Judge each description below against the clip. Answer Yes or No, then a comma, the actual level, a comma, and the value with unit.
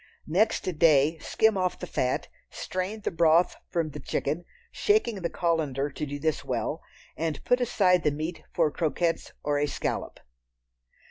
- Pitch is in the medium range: Yes, medium, 165 Hz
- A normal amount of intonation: Yes, average, 3.5 semitones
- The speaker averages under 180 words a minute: Yes, average, 155 wpm